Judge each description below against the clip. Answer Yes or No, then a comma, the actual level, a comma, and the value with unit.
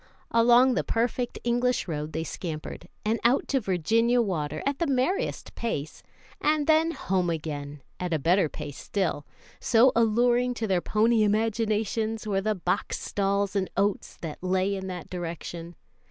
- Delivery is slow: No, average, 155 wpm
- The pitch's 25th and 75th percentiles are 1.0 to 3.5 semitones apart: No, wide, 5.4 semitones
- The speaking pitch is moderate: No, high, 205 Hz